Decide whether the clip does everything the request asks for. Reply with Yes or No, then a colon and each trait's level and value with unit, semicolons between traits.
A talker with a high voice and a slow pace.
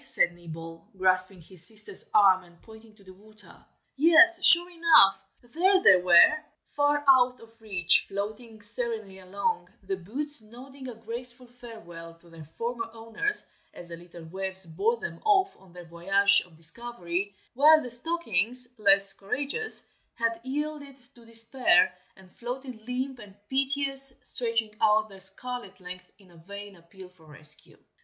No: high, 220 Hz; average, 150 wpm